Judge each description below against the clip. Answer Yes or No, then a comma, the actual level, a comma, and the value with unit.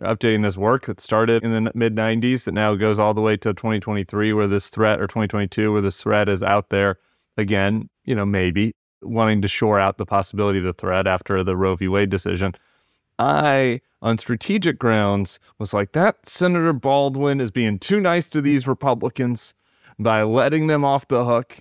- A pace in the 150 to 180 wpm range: No, average, 190 wpm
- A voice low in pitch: Yes, low, 110 Hz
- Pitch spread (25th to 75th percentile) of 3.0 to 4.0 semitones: Yes, average, 3.3 semitones